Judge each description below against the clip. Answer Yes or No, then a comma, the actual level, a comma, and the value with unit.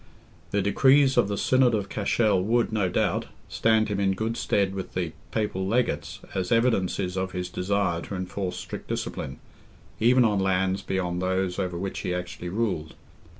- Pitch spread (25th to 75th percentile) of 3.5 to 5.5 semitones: No, average, 3.1 semitones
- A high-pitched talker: No, very low, 95 Hz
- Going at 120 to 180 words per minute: Yes, average, 170 wpm